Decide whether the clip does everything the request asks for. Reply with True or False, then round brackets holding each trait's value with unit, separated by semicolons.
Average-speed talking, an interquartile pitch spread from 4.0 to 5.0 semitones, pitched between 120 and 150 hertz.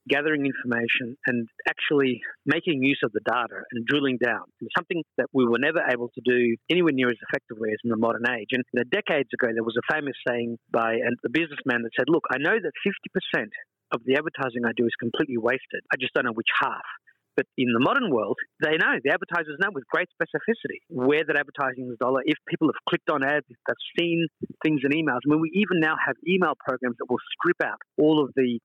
False (220 wpm; 4.5 semitones; 135 Hz)